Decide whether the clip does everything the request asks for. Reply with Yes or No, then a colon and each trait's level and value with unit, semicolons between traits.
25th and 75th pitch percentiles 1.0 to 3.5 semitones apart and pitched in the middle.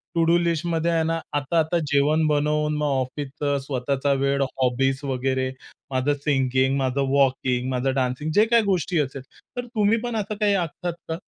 No: average, 4.0 semitones; medium, 145 Hz